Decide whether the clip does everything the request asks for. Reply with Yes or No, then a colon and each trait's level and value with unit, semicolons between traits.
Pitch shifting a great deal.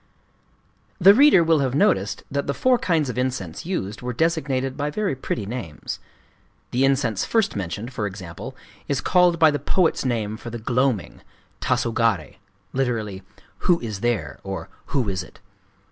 Yes: wide, 6.1 semitones